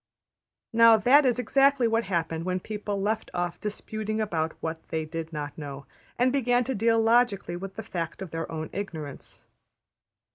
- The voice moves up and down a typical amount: No, wide, 5.8 semitones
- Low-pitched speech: No, high, 200 Hz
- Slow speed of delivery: No, average, 175 wpm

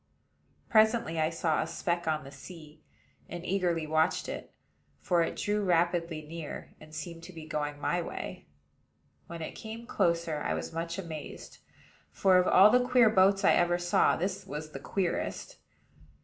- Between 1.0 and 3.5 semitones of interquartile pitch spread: Yes, average, 3.0 semitones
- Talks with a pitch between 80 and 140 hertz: No, medium, 170 Hz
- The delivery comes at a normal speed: Yes, average, 165 wpm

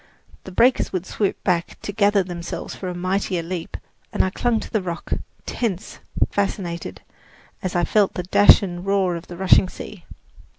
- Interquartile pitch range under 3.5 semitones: Yes, narrow, 2.4 semitones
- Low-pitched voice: No, medium, 185 Hz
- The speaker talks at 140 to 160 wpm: No, average, 175 wpm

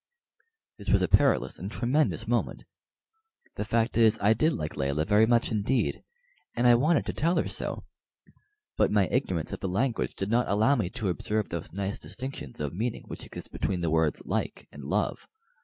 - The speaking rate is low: No, average, 190 wpm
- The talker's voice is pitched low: Yes, low, 105 Hz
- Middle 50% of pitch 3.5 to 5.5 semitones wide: Yes, average, 5.1 semitones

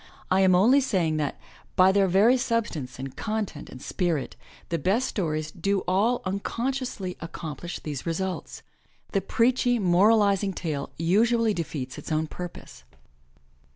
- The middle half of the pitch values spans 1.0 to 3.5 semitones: No, average, 5.1 semitones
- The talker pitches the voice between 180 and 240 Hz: Yes, medium, 185 Hz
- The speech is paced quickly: No, slow, 135 wpm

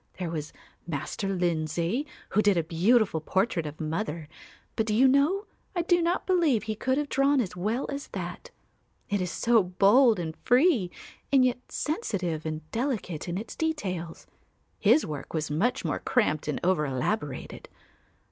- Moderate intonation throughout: No, wide, 8.0 semitones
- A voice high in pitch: Yes, high, 200 Hz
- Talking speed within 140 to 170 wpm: Yes, average, 165 wpm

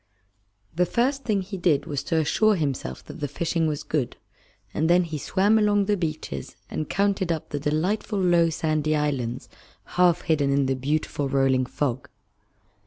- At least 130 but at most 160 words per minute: No, average, 170 wpm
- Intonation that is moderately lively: Yes, average, 4.3 semitones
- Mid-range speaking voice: Yes, medium, 155 Hz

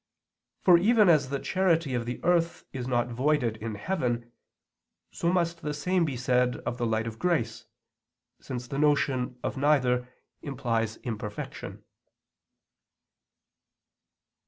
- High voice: No, low, 130 Hz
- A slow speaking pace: Yes, slow, 130 wpm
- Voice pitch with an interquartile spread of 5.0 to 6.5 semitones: Yes, wide, 5.6 semitones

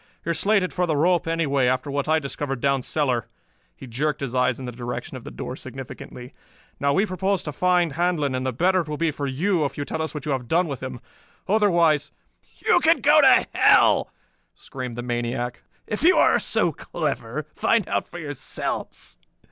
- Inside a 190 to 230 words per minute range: Yes, fast, 205 wpm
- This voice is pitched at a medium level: Yes, medium, 145 Hz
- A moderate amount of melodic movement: Yes, average, 4.8 semitones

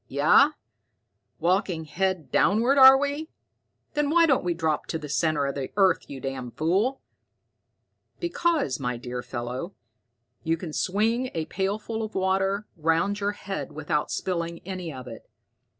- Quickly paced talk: No, average, 150 wpm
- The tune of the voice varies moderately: No, wide, 6.3 semitones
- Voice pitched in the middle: Yes, medium, 180 Hz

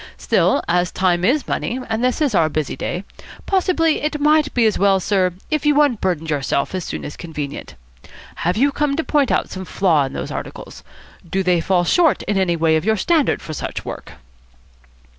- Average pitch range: No, wide, 8.9 semitones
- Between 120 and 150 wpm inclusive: No, average, 200 wpm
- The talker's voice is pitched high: Yes, high, 195 Hz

